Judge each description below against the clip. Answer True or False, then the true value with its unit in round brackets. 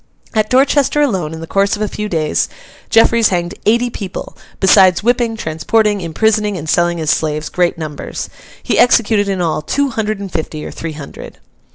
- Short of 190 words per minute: True (180 wpm)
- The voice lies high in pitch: True (195 Hz)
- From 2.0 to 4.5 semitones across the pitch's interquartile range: False (5.3 semitones)